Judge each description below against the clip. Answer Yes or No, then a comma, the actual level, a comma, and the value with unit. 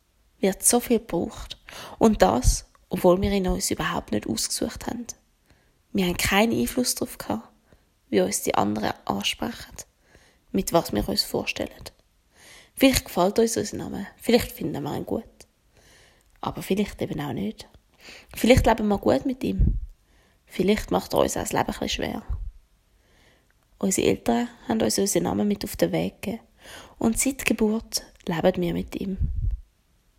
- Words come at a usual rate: Yes, average, 155 wpm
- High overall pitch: Yes, high, 195 Hz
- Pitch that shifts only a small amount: No, average, 5.2 semitones